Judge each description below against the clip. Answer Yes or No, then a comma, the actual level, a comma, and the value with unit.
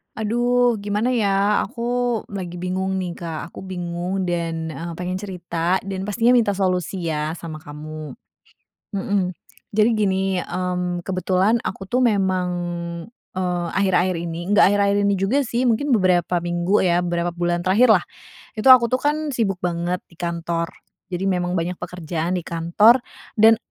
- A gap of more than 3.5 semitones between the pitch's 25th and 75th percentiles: No, average, 3.1 semitones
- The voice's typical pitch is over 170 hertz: Yes, medium, 185 Hz